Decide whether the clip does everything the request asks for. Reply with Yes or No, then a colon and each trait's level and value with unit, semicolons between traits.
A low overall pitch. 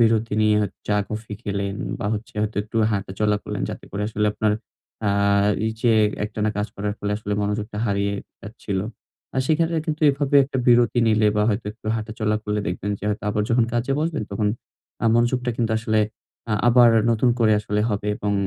Yes: low, 110 Hz